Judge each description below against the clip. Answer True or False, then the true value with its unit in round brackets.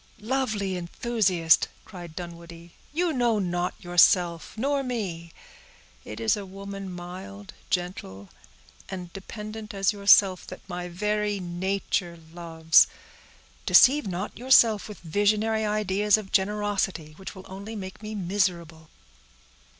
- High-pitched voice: True (195 Hz)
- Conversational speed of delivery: False (120 wpm)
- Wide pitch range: False (3.2 semitones)